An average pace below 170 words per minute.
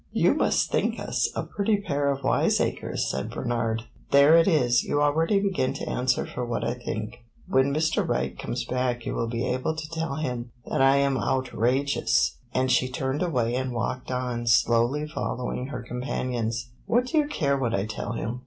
No: average, 190 wpm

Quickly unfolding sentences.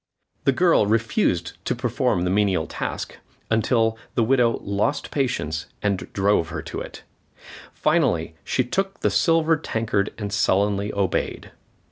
No: slow, 135 wpm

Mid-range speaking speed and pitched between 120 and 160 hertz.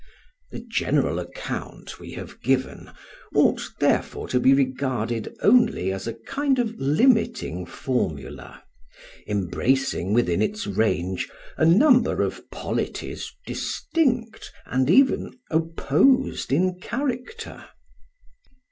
No: slow, 105 wpm; medium, 140 Hz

